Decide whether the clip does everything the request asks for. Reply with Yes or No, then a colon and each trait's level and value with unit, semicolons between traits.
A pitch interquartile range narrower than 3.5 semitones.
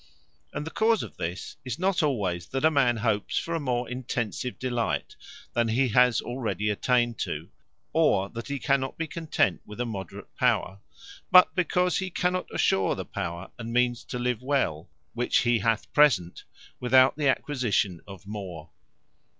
No: average, 4.9 semitones